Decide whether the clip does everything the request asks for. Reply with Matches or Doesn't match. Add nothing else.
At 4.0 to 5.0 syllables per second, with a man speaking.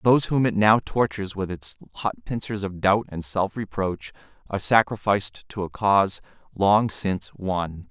Matches